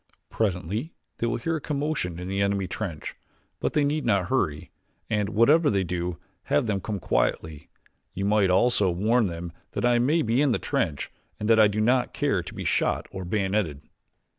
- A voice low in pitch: Yes, low, 105 Hz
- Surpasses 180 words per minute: Yes, average, 190 wpm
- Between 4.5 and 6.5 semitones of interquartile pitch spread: Yes, average, 5.2 semitones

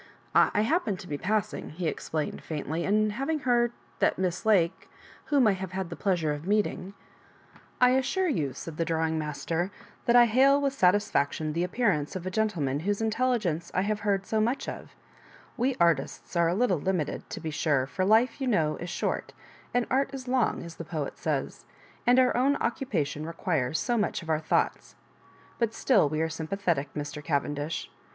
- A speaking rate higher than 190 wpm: Yes, average, 200 wpm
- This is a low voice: No, medium, 185 Hz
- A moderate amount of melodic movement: No, wide, 6.6 semitones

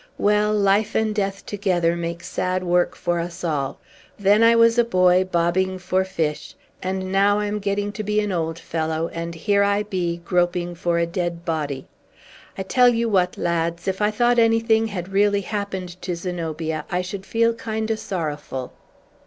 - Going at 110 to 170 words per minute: No, average, 180 wpm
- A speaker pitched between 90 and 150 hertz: No, medium, 185 Hz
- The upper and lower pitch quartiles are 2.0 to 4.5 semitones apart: Yes, average, 3.4 semitones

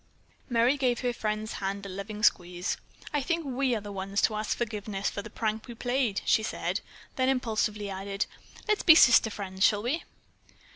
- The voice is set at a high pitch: Yes, high, 215 Hz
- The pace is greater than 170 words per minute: Yes, average, 185 wpm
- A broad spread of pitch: No, average, 3.6 semitones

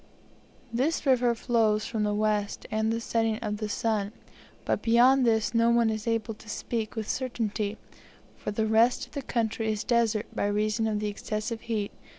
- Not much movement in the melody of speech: Yes, narrow, 1.7 semitones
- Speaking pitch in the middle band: No, high, 220 Hz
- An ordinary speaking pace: Yes, average, 180 wpm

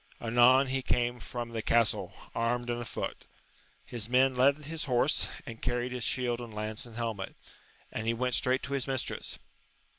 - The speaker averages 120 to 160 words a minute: No, average, 175 wpm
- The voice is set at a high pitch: No, low, 120 Hz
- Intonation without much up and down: Yes, narrow, 1.7 semitones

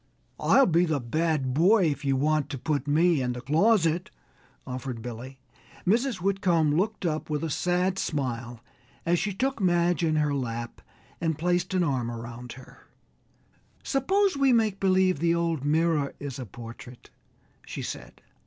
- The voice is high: No, medium, 160 Hz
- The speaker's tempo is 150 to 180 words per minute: Yes, average, 160 wpm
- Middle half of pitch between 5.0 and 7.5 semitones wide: Yes, wide, 5.6 semitones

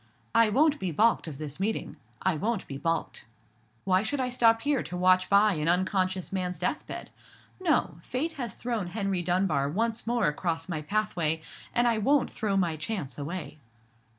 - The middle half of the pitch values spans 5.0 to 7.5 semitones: Yes, wide, 5.6 semitones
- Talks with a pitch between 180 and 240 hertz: Yes, high, 190 Hz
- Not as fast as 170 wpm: No, average, 175 wpm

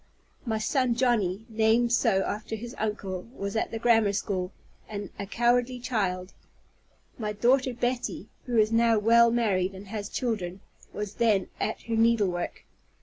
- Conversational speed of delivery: Yes, average, 150 wpm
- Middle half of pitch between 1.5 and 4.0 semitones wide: Yes, average, 2.9 semitones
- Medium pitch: No, high, 220 Hz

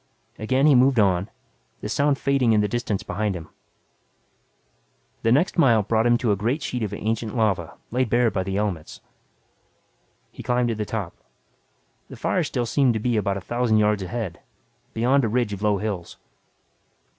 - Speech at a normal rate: Yes, average, 180 wpm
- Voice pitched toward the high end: No, low, 110 Hz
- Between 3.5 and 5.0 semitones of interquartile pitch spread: No, average, 3.1 semitones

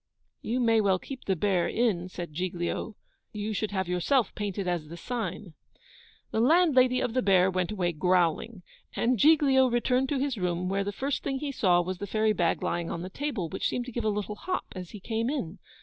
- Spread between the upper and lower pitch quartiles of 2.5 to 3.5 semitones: No, wide, 5.6 semitones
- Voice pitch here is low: No, high, 205 Hz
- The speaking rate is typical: No, fast, 210 wpm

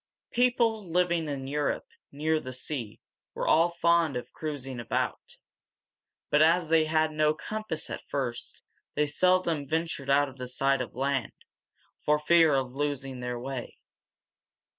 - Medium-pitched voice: Yes, medium, 150 Hz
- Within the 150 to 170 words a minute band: No, average, 140 wpm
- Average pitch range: Yes, average, 3.4 semitones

